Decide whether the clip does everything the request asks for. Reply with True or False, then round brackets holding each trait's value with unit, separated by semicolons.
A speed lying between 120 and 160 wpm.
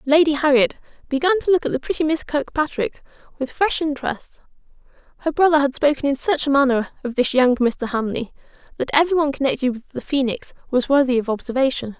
False (185 wpm)